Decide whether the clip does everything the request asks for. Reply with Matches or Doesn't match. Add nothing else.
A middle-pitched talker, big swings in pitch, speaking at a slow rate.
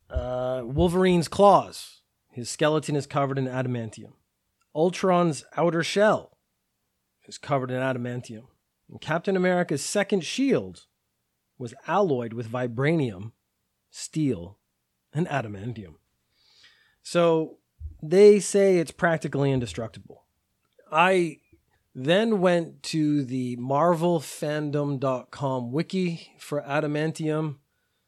Matches